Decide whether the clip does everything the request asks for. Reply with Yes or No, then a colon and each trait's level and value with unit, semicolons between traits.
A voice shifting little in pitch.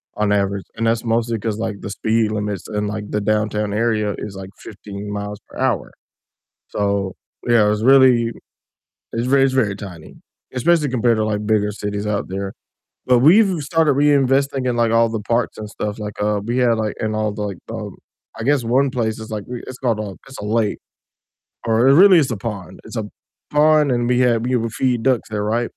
No: average, 3.2 semitones